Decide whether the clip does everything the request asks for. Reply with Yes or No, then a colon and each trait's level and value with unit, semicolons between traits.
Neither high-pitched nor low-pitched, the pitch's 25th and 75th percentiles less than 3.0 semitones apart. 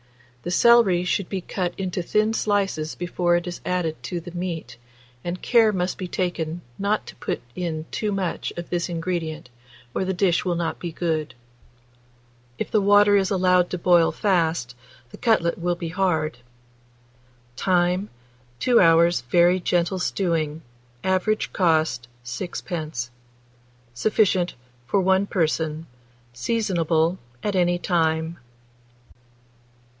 Yes: medium, 175 Hz; narrow, 2.4 semitones